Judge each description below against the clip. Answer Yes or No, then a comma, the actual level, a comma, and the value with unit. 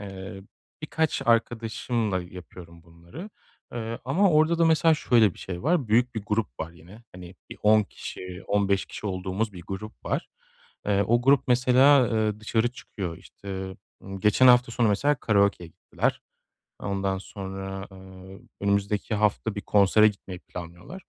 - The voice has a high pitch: No, low, 105 Hz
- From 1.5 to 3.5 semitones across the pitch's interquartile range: No, average, 4.0 semitones